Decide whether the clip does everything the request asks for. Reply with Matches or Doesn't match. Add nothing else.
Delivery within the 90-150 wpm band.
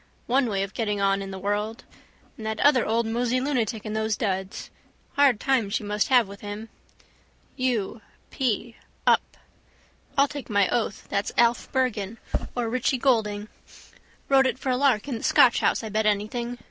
Doesn't match